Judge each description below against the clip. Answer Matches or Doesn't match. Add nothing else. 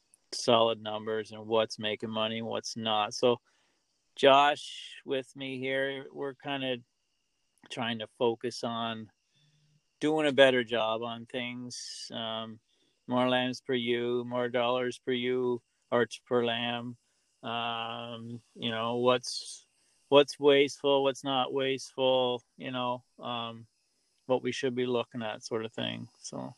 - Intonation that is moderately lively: Doesn't match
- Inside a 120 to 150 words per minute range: Matches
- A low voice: Matches